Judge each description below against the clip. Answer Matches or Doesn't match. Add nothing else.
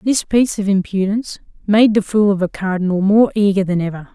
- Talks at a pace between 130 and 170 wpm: Doesn't match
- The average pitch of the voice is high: Matches